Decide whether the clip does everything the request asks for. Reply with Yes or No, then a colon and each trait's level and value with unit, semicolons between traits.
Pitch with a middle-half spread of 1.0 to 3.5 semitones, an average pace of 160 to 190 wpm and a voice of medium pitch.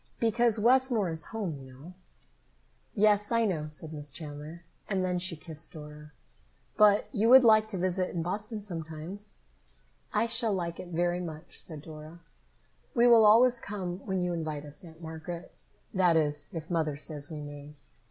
No: average, 5.1 semitones; average, 170 wpm; medium, 175 Hz